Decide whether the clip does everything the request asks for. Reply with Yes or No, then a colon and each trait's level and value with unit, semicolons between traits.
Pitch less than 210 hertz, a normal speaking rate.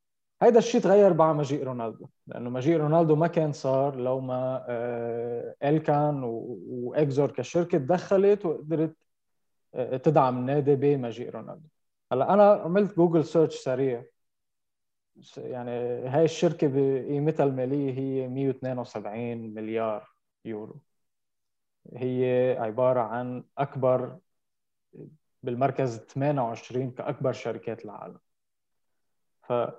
Yes: low, 135 Hz; average, 95 wpm